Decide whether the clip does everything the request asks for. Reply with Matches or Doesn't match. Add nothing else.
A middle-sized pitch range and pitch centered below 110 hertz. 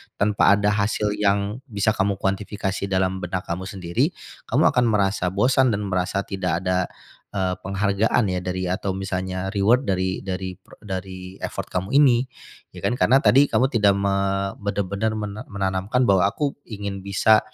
Doesn't match